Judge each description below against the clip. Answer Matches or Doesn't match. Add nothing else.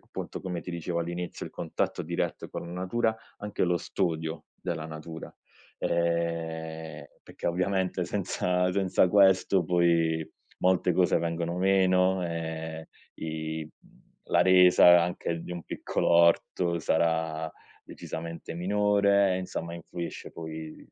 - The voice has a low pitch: Matches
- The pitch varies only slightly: Matches